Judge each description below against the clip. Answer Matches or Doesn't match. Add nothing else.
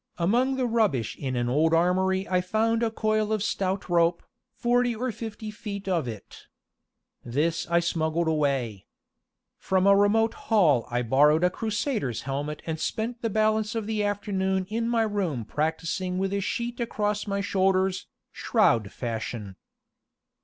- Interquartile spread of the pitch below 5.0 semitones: Doesn't match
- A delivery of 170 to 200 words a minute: Doesn't match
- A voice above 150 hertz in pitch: Matches